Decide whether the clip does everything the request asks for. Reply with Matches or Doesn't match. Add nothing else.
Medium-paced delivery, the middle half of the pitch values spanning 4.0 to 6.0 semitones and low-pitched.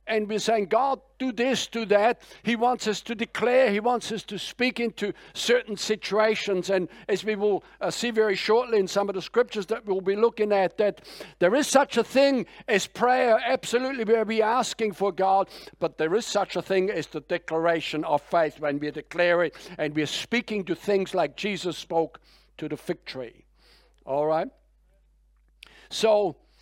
Doesn't match